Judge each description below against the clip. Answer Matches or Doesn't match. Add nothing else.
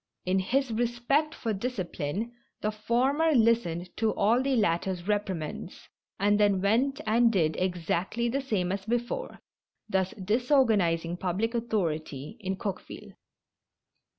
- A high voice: Matches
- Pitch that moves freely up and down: Doesn't match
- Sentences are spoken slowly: Matches